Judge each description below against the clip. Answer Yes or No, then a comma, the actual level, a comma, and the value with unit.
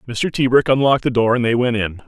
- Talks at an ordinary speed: No, fast, 260 wpm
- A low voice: Yes, low, 120 Hz